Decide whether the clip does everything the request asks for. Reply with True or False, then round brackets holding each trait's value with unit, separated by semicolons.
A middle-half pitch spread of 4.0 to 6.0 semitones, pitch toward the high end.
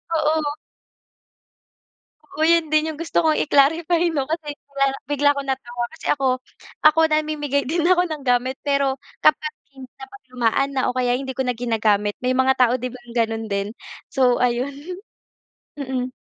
False (3.6 semitones; 270 Hz)